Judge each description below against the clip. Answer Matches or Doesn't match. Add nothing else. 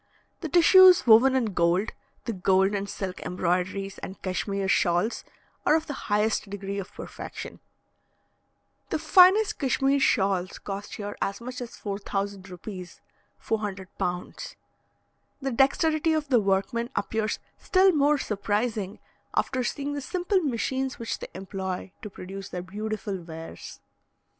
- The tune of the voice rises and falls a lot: Matches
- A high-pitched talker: Matches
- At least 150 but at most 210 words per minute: Doesn't match